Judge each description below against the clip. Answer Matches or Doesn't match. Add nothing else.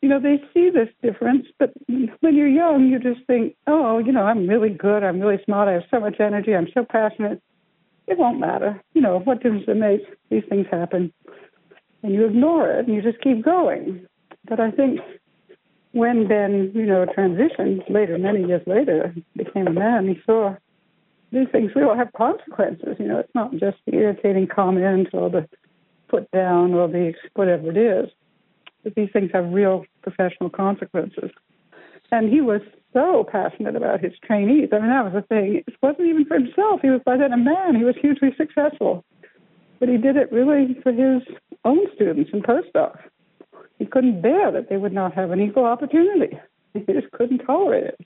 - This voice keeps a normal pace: Matches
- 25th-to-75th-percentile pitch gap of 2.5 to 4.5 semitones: Doesn't match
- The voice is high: Matches